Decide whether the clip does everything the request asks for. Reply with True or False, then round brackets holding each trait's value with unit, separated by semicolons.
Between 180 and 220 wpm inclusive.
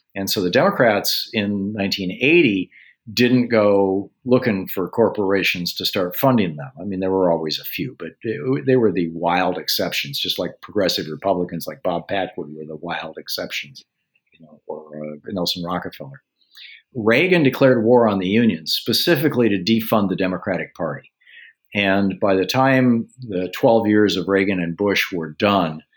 False (160 wpm)